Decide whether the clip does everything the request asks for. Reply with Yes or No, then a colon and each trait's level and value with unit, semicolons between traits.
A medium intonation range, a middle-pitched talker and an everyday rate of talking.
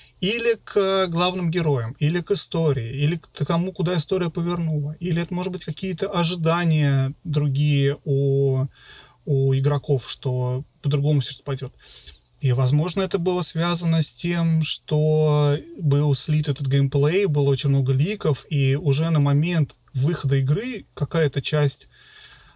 Yes: average, 3.7 semitones; medium, 150 Hz; average, 135 wpm